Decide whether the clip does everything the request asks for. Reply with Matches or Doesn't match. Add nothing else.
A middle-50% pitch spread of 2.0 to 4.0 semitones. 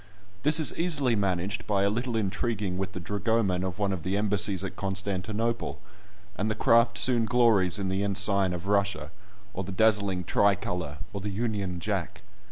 Matches